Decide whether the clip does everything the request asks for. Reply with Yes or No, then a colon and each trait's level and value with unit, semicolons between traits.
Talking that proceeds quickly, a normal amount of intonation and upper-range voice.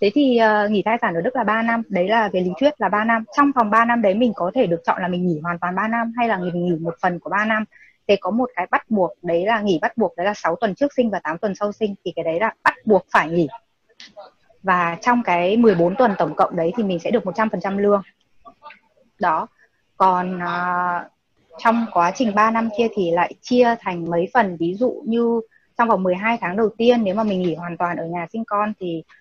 Yes: fast, 255 wpm; average, 4.6 semitones; high, 205 Hz